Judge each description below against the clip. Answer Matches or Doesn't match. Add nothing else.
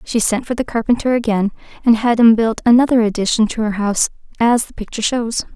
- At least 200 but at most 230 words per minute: Matches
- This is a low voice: Doesn't match